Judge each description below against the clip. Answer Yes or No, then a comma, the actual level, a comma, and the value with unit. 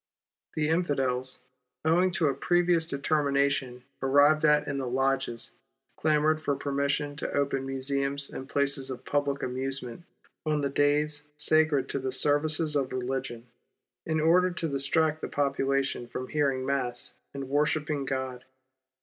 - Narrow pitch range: Yes, narrow, 2.2 semitones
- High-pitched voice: No, medium, 140 Hz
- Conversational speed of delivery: Yes, average, 150 wpm